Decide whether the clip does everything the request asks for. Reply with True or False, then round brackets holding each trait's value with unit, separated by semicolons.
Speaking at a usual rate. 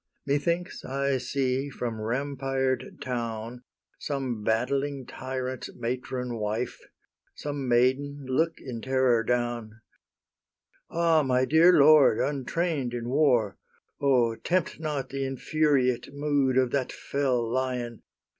False (110 wpm)